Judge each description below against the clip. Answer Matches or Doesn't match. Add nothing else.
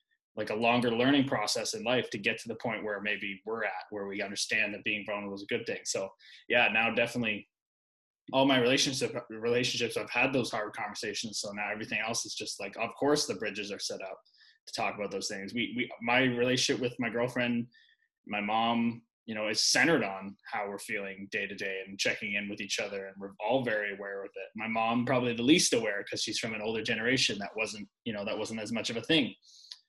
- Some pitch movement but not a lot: Matches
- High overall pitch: Doesn't match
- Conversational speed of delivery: Doesn't match